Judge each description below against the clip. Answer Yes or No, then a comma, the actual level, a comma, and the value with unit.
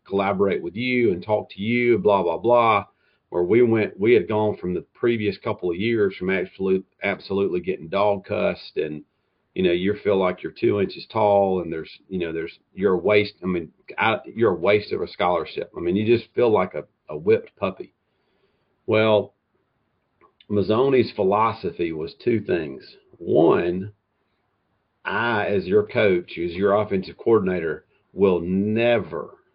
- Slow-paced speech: No, average, 165 wpm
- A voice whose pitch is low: Yes, low, 100 Hz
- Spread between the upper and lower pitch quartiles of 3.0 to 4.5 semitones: No, narrow, 2.4 semitones